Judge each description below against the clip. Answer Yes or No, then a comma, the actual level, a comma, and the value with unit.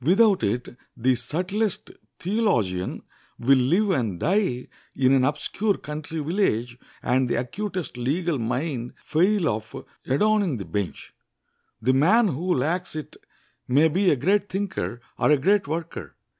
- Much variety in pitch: Yes, wide, 7.3 semitones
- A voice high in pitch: No, medium, 150 Hz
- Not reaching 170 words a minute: Yes, average, 140 wpm